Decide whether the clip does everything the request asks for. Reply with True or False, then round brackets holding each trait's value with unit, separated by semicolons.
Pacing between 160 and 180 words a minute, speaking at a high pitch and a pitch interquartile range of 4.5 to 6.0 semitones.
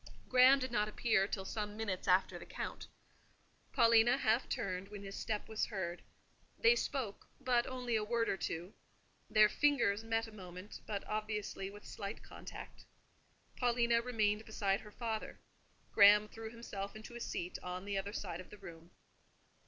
False (165 wpm; 210 Hz; 2.8 semitones)